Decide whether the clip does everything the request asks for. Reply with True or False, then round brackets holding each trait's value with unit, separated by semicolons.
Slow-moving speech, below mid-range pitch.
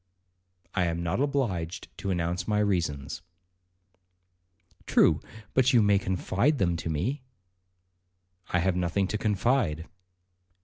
True (120 wpm; 95 Hz)